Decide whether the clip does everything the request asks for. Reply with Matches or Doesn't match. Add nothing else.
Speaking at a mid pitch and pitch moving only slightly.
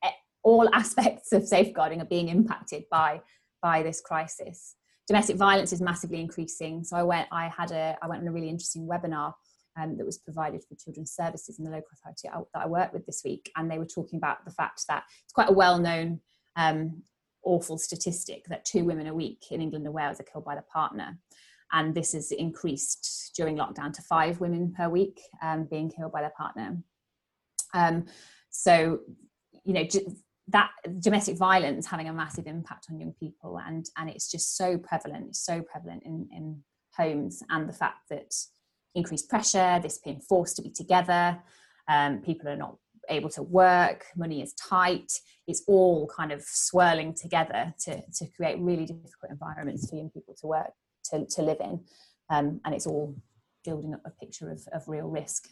Matches